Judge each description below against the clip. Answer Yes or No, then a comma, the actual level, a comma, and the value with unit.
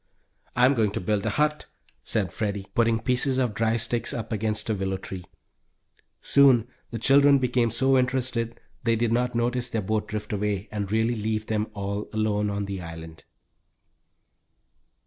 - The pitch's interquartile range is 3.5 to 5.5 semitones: No, average, 2.9 semitones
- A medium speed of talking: Yes, average, 165 wpm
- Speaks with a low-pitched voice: Yes, low, 110 Hz